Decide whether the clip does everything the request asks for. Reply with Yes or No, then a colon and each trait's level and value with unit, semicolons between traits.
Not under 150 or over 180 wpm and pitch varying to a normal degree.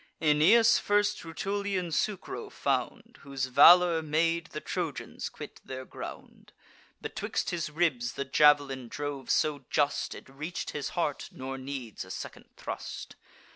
No: slow, 135 wpm; average, 4.2 semitones